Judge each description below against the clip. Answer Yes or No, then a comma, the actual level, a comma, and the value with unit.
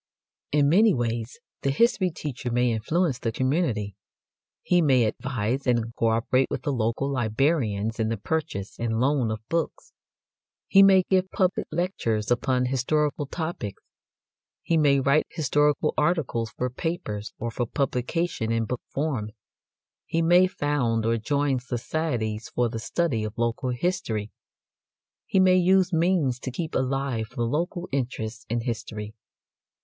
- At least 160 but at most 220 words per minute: No, average, 145 wpm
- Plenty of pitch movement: Yes, wide, 5.8 semitones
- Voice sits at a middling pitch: No, low, 130 Hz